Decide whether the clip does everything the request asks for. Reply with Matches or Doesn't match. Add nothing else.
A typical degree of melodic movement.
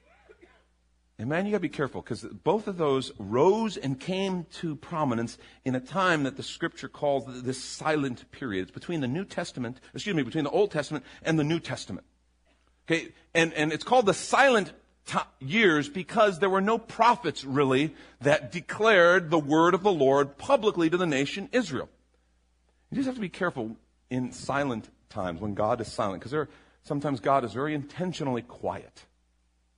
Doesn't match